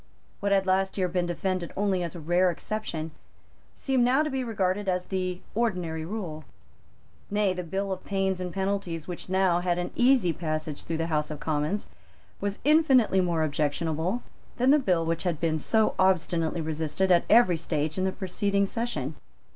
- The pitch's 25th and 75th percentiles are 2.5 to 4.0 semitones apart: Yes, average, 3.4 semitones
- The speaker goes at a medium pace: Yes, average, 180 wpm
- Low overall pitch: No, medium, 185 Hz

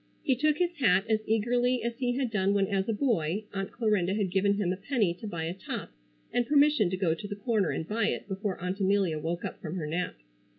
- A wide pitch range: No, average, 4.2 semitones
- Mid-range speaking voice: No, high, 205 Hz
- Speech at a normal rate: No, fast, 245 wpm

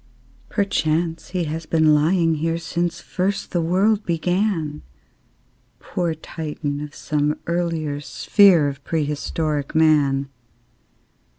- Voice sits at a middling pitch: Yes, medium, 160 Hz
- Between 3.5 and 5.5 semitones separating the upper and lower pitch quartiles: No, average, 2.7 semitones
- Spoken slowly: Yes, slow, 105 wpm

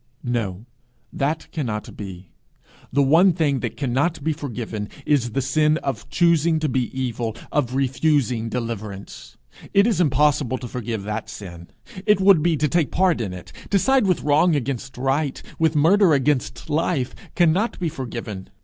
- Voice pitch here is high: No, medium, 140 Hz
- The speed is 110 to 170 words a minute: Yes, average, 160 wpm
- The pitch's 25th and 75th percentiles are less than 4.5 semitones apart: No, average, 5.3 semitones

